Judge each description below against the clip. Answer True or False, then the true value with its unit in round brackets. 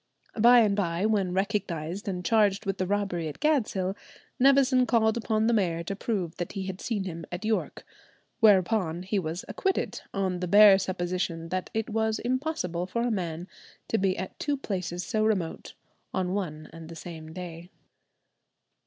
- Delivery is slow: False (170 wpm)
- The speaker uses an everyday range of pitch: True (3.8 semitones)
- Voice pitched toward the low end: False (190 Hz)